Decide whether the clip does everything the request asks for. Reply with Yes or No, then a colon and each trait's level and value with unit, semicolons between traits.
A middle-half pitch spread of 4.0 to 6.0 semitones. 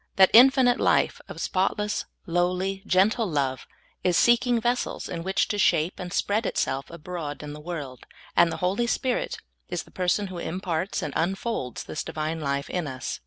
Yes: average, 4.8 semitones